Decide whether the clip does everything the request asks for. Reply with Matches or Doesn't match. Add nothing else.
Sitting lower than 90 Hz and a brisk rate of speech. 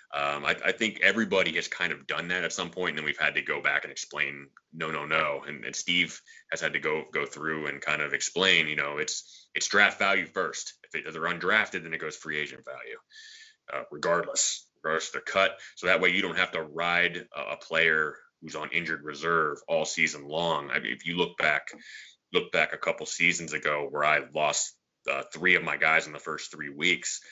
Matches